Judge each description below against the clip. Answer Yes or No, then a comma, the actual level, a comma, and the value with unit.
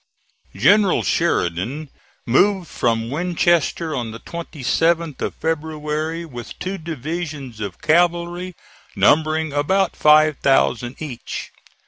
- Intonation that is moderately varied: Yes, average, 4.3 semitones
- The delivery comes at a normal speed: No, slow, 100 wpm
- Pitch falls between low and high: Yes, medium, 155 Hz